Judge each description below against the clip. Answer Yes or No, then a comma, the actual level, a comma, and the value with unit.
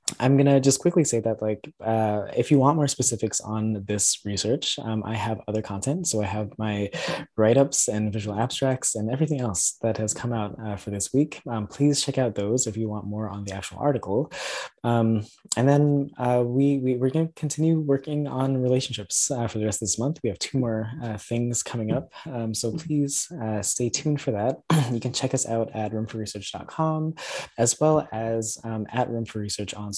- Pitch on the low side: Yes, low, 115 Hz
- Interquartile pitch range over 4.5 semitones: No, average, 4.2 semitones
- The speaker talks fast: Yes, fast, 210 wpm